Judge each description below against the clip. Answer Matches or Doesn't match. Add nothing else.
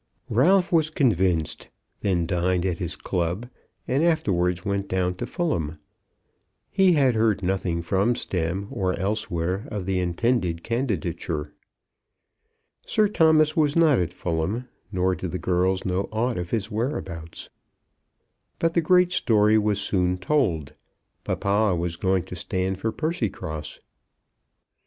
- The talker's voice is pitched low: Matches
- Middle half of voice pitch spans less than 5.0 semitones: Doesn't match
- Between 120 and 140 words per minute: Matches